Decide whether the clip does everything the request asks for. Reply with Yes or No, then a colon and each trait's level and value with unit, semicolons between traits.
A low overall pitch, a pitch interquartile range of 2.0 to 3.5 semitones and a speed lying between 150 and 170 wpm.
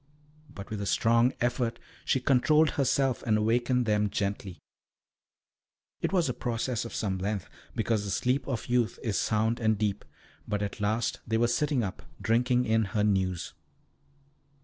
Yes: low, 115 Hz; average, 3.1 semitones; average, 160 wpm